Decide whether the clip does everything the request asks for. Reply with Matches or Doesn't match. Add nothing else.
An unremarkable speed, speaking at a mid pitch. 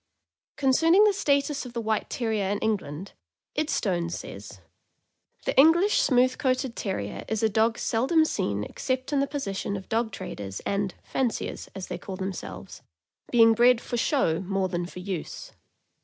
Doesn't match